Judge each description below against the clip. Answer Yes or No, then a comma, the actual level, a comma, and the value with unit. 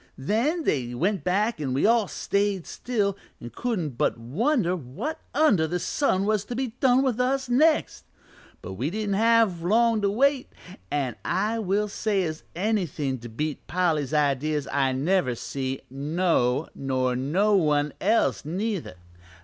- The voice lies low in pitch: No, medium, 185 Hz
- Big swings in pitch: Yes, wide, 7.8 semitones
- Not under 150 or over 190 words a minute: Yes, average, 155 wpm